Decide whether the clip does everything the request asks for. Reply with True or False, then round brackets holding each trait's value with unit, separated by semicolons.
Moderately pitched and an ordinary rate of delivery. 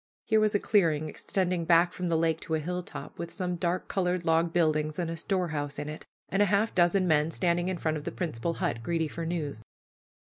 False (170 Hz; 220 wpm)